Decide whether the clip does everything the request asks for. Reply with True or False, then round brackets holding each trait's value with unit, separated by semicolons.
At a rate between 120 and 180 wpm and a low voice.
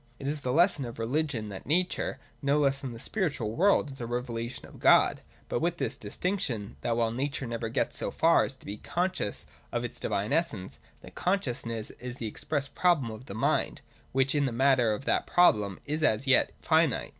False (205 wpm; 130 Hz)